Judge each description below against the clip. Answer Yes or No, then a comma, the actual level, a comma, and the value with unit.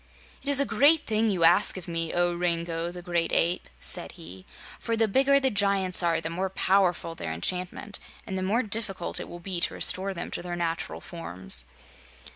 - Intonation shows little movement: No, average, 3.4 semitones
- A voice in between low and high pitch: Yes, medium, 180 Hz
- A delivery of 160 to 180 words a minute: No, average, 200 wpm